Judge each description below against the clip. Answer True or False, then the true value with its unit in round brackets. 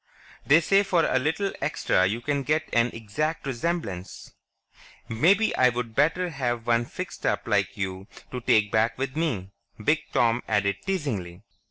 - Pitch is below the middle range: True (125 Hz)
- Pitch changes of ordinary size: False (6.5 semitones)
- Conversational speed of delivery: True (155 wpm)